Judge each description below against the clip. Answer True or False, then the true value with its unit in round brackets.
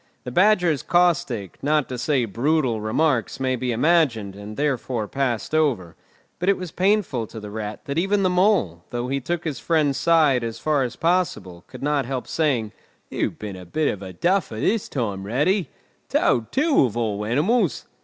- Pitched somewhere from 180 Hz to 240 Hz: False (135 Hz)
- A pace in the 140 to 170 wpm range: False (185 wpm)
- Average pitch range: False (6.9 semitones)